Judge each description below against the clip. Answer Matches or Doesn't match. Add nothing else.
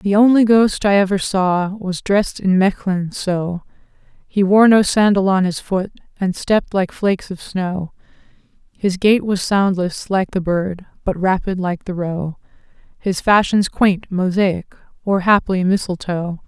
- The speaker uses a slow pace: Doesn't match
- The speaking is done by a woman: Matches